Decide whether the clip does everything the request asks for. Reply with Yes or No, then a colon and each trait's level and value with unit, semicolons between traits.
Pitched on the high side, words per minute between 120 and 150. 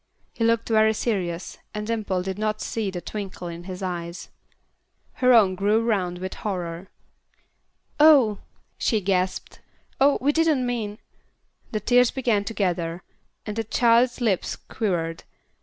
Yes: high, 210 Hz; average, 145 wpm